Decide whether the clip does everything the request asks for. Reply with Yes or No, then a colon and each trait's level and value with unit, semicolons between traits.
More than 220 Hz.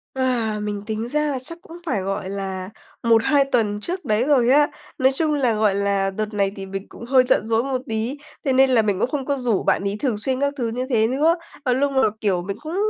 Yes: high, 235 Hz